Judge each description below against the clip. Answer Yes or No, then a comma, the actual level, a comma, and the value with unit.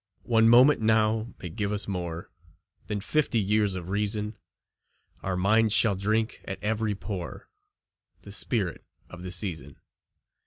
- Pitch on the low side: Yes, low, 105 Hz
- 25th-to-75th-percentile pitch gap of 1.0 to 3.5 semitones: Yes, average, 2.9 semitones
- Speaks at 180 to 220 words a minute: No, average, 140 wpm